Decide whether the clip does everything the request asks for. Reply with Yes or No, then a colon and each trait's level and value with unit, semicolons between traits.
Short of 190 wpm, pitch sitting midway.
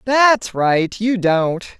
No: slow, 135 wpm; high, 205 Hz